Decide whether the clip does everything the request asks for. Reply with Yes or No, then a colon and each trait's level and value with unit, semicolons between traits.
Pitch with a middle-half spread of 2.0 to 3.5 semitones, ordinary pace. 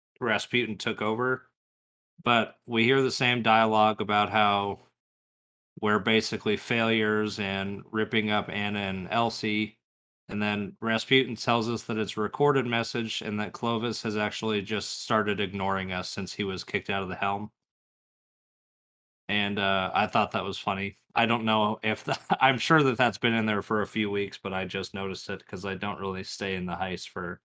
Yes: narrow, 2.5 semitones; average, 185 wpm